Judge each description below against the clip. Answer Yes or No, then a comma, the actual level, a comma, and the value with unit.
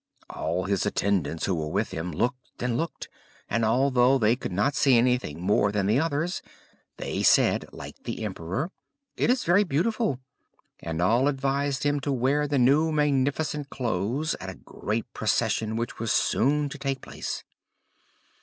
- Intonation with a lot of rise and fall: Yes, wide, 5.7 semitones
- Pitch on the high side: No, low, 125 Hz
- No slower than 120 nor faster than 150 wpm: No, average, 165 wpm